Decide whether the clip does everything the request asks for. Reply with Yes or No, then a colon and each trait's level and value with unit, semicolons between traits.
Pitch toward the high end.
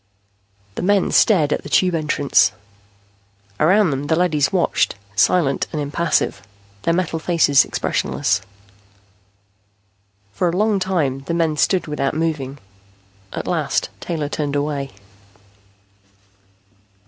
No: medium, 155 Hz